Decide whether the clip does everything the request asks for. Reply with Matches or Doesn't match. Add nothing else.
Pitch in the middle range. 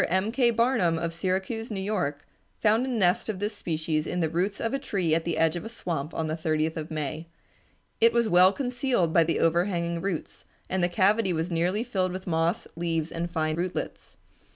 Matches